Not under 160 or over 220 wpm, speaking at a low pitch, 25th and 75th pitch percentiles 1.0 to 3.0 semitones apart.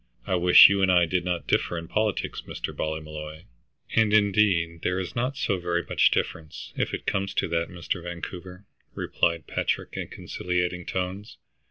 Yes: average, 170 wpm; very low, 90 Hz; narrow, 2.5 semitones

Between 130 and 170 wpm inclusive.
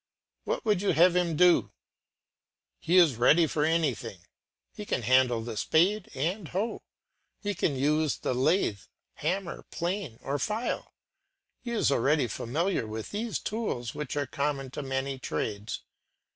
Yes: average, 145 wpm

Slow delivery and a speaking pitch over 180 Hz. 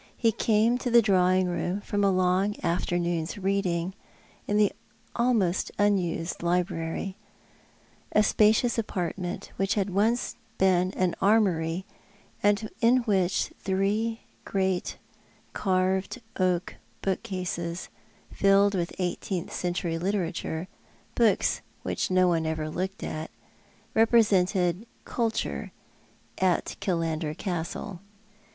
Yes: slow, 105 wpm; high, 190 Hz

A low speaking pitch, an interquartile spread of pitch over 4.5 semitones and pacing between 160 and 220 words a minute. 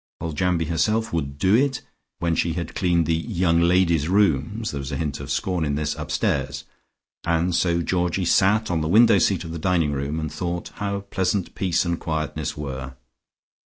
No: very low, 85 Hz; average, 3.2 semitones; average, 185 wpm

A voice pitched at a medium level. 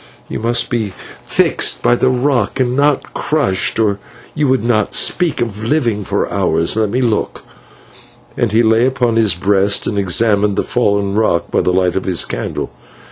No: low, 110 Hz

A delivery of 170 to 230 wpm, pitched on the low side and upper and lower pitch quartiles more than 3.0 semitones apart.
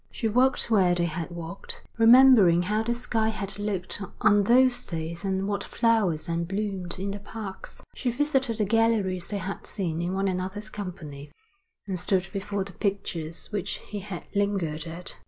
No: average, 175 wpm; high, 195 Hz; average, 3.5 semitones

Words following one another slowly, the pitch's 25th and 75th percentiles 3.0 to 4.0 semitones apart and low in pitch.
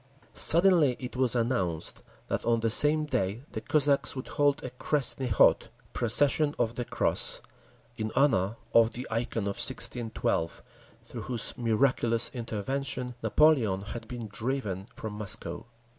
Yes: slow, 130 wpm; average, 3.6 semitones; low, 120 Hz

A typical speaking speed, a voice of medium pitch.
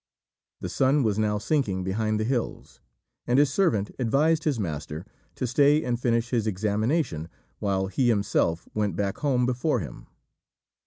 No: average, 155 wpm; low, 115 Hz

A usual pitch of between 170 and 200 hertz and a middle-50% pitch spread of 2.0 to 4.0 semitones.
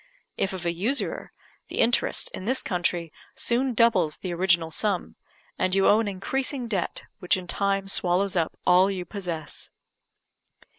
Yes: high, 190 Hz; average, 3.2 semitones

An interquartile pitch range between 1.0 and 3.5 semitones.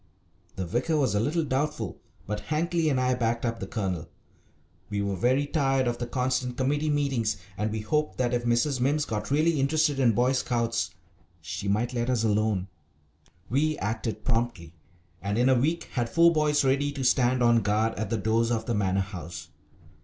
No: average, 4.3 semitones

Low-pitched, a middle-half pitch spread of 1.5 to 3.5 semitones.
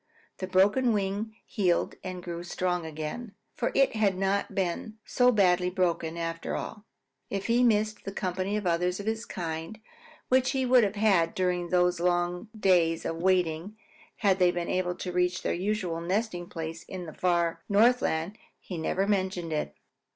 No: medium, 185 Hz; average, 3.2 semitones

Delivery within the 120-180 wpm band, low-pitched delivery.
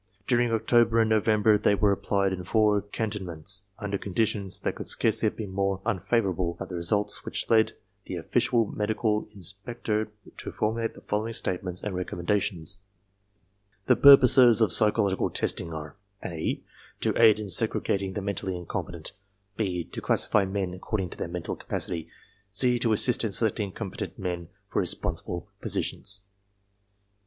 Yes: average, 160 wpm; low, 100 Hz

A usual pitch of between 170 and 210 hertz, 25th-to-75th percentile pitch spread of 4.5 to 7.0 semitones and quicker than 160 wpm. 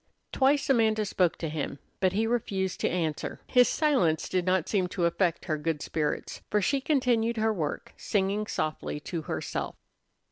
Yes: high, 190 Hz; average, 5.3 semitones; average, 170 wpm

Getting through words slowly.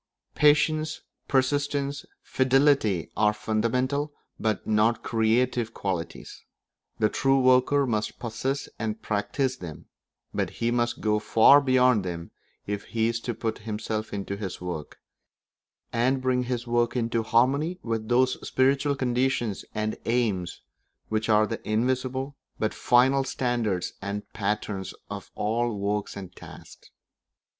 Yes: slow, 130 wpm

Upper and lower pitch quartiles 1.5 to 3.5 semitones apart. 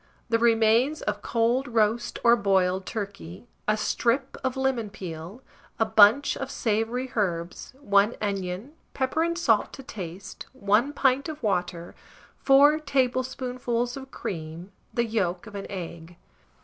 No: average, 4.7 semitones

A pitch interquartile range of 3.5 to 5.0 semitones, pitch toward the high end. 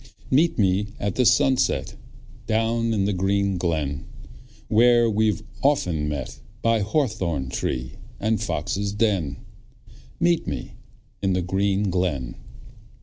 No: average, 4.1 semitones; low, 100 Hz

